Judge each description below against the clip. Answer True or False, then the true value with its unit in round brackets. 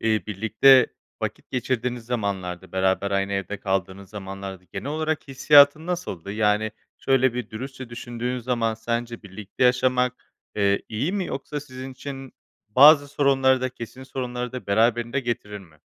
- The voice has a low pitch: True (120 Hz)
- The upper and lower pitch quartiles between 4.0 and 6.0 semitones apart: True (4.4 semitones)